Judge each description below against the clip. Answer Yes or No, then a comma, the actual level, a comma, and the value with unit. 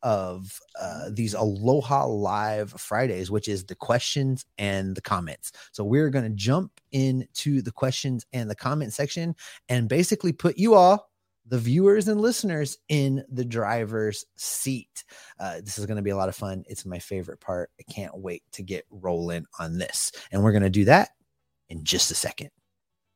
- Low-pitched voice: Yes, low, 115 Hz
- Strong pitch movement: Yes, wide, 5.9 semitones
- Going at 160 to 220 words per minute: Yes, average, 175 wpm